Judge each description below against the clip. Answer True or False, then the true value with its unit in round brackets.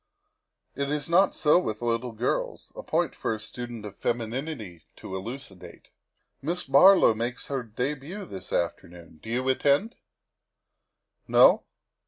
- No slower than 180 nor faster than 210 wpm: False (135 wpm)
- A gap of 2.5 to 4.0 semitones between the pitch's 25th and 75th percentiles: False (5.1 semitones)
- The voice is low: True (125 Hz)